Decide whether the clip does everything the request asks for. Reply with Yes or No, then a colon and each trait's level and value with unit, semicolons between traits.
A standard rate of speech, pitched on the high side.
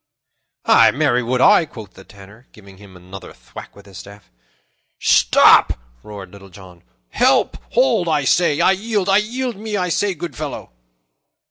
No: average, 165 wpm; low, 125 Hz